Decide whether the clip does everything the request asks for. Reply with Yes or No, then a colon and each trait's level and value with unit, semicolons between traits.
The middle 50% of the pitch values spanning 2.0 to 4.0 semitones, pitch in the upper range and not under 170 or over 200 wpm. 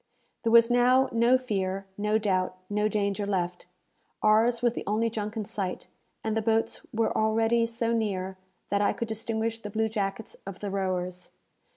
Yes: narrow, 2.5 semitones; high, 215 Hz; average, 175 wpm